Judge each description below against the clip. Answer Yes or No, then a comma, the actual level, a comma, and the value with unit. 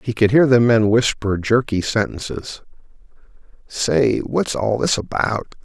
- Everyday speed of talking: No, slow, 115 wpm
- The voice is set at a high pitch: No, low, 115 Hz